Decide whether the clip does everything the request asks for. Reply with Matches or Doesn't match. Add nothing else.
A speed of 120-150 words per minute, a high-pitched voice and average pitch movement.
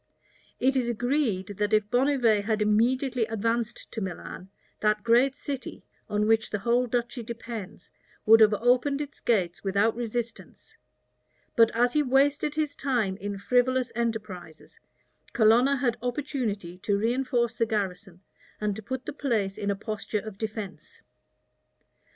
Matches